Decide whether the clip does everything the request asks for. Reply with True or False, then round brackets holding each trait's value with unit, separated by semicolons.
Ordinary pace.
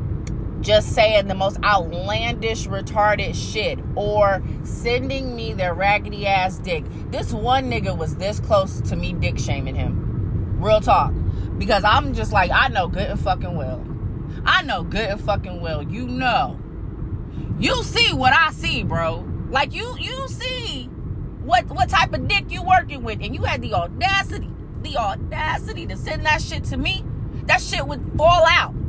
True (170 wpm)